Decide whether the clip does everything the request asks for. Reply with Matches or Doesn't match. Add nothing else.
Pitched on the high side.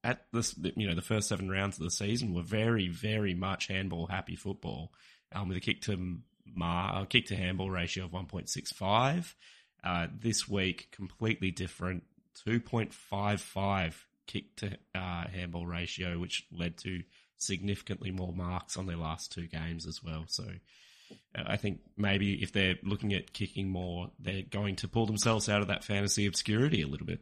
Doesn't match